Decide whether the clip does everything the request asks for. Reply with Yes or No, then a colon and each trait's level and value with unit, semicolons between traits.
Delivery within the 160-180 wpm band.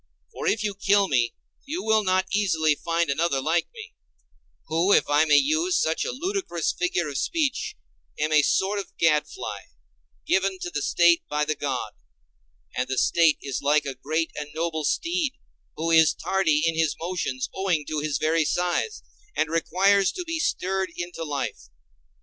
Yes: average, 175 wpm